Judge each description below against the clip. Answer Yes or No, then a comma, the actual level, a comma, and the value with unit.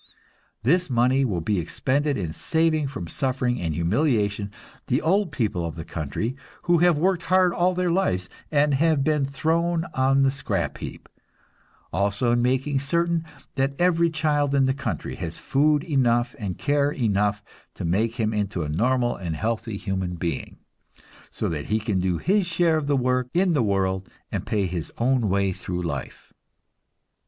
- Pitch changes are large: Yes, wide, 7.3 semitones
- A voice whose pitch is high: No, low, 125 Hz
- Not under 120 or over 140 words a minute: No, average, 170 wpm